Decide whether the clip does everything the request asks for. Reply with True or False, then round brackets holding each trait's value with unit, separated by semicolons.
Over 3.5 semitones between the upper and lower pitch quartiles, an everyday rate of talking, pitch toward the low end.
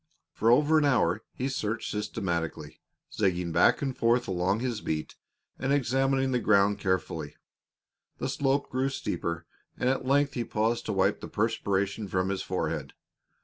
True (5.5 semitones; 155 wpm; 110 Hz)